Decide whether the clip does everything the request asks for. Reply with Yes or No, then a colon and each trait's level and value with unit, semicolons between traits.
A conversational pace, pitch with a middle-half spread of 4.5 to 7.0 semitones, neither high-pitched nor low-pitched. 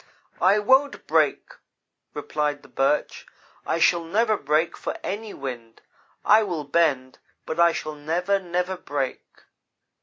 No: slow, 130 wpm; average, 5.2 semitones; medium, 170 Hz